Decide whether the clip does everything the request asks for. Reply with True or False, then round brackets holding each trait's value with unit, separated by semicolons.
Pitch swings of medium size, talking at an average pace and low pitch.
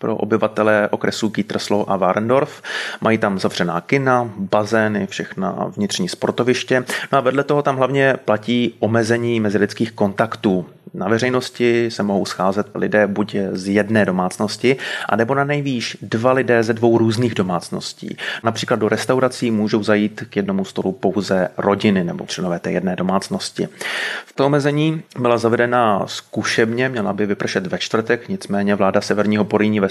True (3.2 semitones; 145 wpm; 115 Hz)